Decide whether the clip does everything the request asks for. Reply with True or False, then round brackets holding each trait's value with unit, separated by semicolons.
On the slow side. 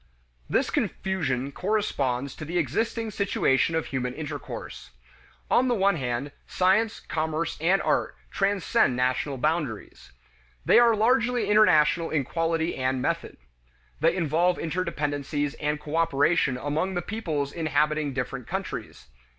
True (125 wpm)